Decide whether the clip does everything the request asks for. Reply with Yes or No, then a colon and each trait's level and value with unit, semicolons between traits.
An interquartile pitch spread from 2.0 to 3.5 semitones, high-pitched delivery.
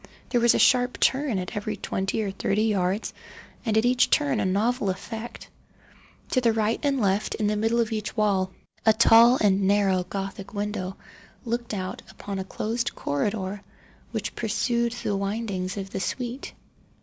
Yes: average, 3.2 semitones; high, 215 Hz